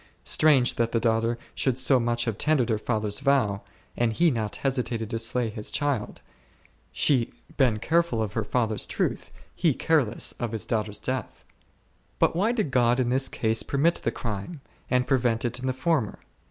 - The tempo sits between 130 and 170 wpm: No, average, 180 wpm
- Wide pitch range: No, average, 3.4 semitones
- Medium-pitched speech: No, low, 120 Hz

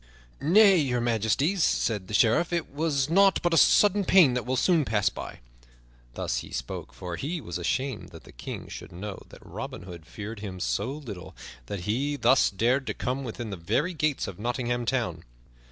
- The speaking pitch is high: No, low, 125 Hz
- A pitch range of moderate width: No, wide, 6.8 semitones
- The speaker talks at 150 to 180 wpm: No, average, 190 wpm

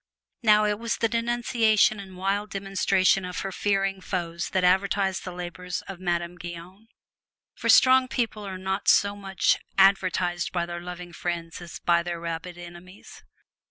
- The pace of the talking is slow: No, average, 160 wpm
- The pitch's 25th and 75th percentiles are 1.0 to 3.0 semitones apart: Yes, narrow, 2.5 semitones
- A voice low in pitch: No, medium, 185 Hz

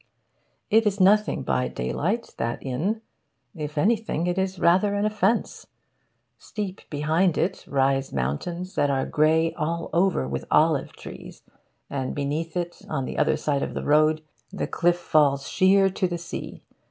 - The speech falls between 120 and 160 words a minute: Yes, average, 155 wpm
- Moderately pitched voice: Yes, medium, 165 Hz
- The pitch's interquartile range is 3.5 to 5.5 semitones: Yes, average, 4.9 semitones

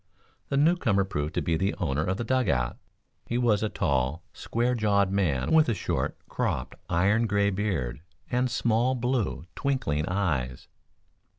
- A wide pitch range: Yes, wide, 7.4 semitones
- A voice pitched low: Yes, low, 100 Hz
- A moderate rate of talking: Yes, average, 160 wpm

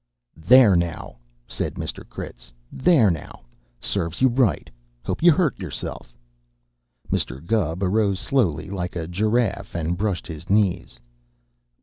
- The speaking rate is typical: No, slow, 125 wpm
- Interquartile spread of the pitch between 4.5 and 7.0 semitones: Yes, average, 4.9 semitones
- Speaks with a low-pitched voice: Yes, low, 100 Hz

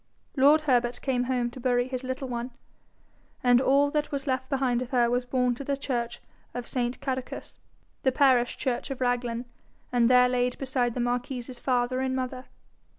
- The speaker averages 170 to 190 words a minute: Yes, average, 180 wpm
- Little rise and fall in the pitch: Yes, narrow, 1.3 semitones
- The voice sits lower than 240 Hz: No, very high, 250 Hz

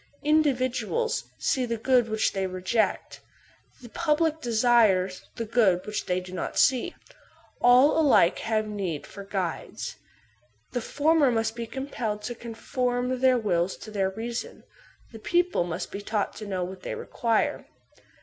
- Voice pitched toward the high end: Yes, high, 230 Hz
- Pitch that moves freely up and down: No, average, 4.4 semitones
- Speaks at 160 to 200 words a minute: No, average, 150 wpm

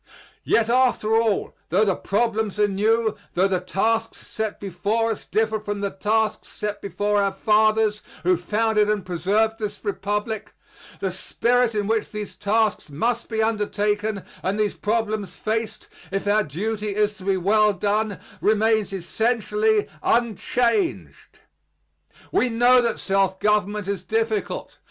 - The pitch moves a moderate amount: No, narrow, 1.8 semitones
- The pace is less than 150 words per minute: Yes, average, 140 wpm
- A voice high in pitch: Yes, high, 210 Hz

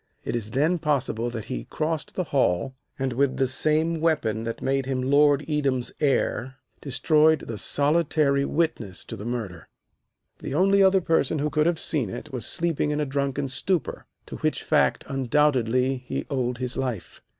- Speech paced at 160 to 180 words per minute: Yes, average, 170 wpm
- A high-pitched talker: No, medium, 140 Hz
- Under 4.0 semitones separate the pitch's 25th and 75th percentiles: Yes, average, 3.4 semitones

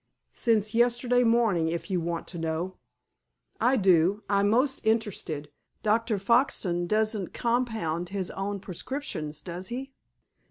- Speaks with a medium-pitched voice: No, high, 205 Hz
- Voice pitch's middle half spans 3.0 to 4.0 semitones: No, average, 5.2 semitones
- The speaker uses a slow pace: Yes, slow, 125 wpm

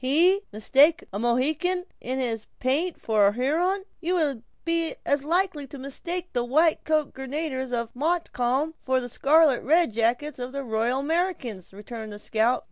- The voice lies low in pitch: No, very high, 270 Hz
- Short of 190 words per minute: Yes, average, 160 wpm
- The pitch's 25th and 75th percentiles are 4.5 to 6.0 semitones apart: Yes, average, 5.2 semitones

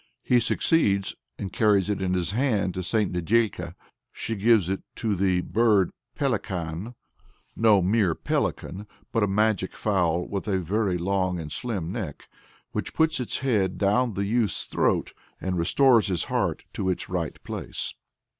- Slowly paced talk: No, average, 155 wpm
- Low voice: Yes, low, 100 Hz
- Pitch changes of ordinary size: Yes, average, 3.4 semitones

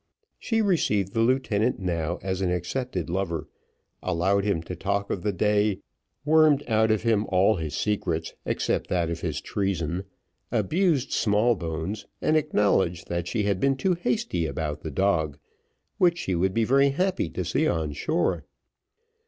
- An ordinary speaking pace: Yes, average, 160 wpm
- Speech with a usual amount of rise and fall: No, wide, 5.8 semitones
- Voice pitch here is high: No, low, 100 Hz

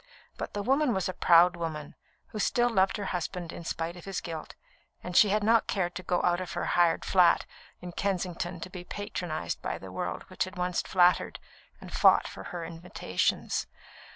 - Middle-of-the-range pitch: Yes, medium, 180 Hz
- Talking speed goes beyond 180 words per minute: Yes, average, 195 wpm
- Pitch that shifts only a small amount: Yes, narrow, 2.2 semitones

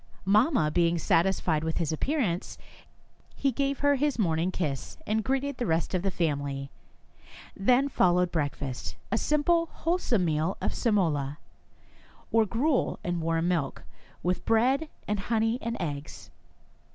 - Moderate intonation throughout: No, wide, 7.6 semitones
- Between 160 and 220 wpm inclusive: No, average, 140 wpm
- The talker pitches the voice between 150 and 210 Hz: Yes, medium, 185 Hz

